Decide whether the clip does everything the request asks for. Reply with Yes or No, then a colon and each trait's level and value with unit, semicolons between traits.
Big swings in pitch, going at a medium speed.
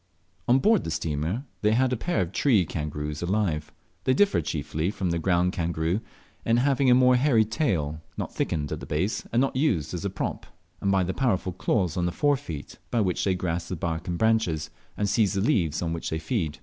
No: wide, 6.4 semitones; fast, 220 wpm